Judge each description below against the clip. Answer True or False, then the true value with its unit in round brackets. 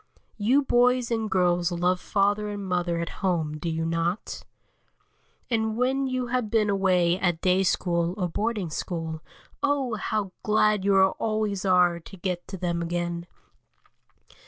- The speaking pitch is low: False (190 Hz)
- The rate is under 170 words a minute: True (150 wpm)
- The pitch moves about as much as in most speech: True (3.9 semitones)